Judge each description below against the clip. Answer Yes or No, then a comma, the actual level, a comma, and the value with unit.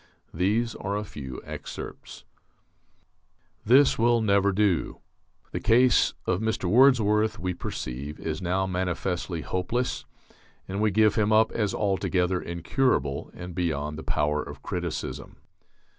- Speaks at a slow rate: Yes, slow, 130 wpm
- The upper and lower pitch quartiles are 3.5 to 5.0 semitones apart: Yes, average, 4.1 semitones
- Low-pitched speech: Yes, very low, 95 Hz